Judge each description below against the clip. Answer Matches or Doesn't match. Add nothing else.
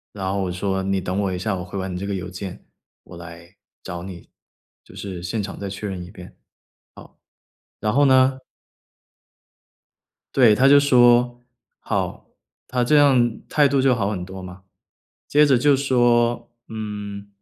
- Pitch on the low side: Matches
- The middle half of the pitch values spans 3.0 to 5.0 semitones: Matches